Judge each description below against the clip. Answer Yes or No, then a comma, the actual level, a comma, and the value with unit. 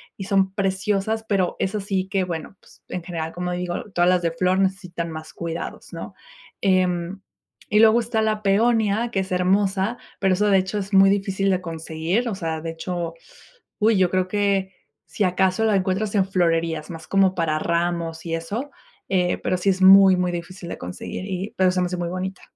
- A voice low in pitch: No, medium, 185 Hz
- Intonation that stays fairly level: Yes, narrow, 2.2 semitones